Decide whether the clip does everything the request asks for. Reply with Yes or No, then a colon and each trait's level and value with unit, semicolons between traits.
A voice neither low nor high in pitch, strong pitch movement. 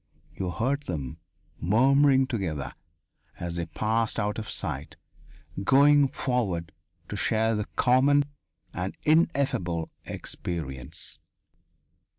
No: low, 110 Hz; wide, 7.6 semitones